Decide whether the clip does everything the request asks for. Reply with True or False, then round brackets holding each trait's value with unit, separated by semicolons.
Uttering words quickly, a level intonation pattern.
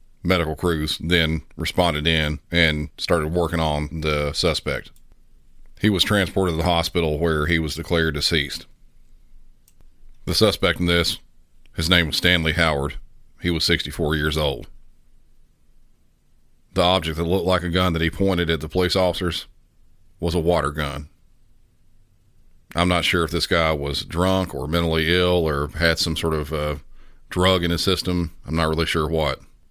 False (160 wpm; 2.3 semitones)